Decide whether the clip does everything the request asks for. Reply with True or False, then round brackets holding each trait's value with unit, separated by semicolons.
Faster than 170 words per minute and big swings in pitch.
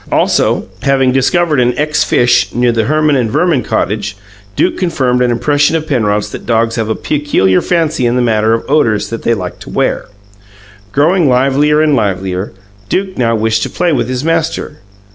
False (180 wpm; 5.0 semitones)